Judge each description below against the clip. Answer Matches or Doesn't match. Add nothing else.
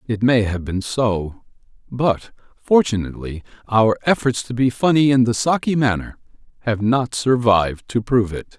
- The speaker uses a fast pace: Doesn't match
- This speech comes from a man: Matches